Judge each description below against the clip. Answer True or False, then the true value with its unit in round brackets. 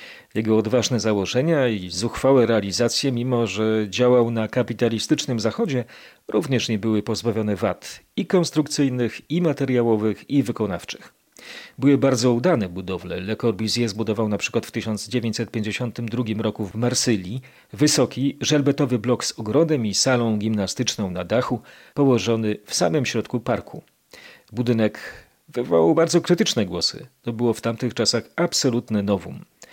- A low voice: True (120 Hz)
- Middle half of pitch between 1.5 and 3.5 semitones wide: True (2.8 semitones)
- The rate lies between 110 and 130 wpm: True (125 wpm)